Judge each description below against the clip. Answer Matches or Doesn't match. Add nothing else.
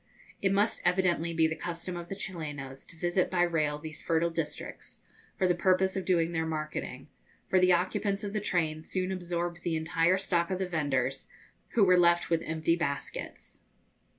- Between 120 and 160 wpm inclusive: Doesn't match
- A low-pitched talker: Doesn't match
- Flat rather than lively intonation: Matches